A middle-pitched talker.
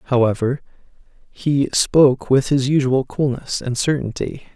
No: low, 130 Hz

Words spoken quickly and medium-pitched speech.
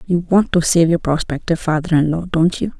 Yes: fast, 235 wpm; medium, 165 Hz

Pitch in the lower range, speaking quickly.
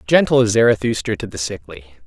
No: low, 105 Hz; average, 175 wpm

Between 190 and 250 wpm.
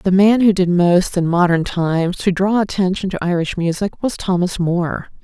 Yes: average, 195 wpm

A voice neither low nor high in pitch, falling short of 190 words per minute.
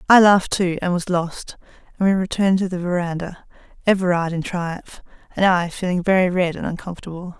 Yes: medium, 180 Hz; average, 170 wpm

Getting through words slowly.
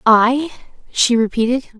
Yes: slow, 100 wpm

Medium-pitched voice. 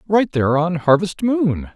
Yes: medium, 170 Hz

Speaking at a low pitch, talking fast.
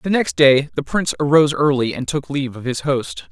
No: medium, 145 Hz; fast, 235 wpm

